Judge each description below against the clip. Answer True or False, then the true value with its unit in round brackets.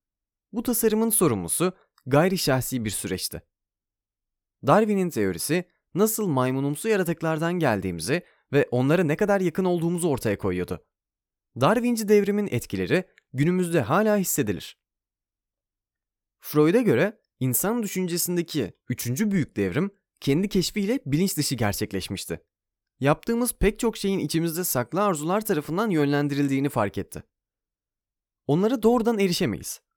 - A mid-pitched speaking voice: True (150 Hz)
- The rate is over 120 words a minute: False (105 wpm)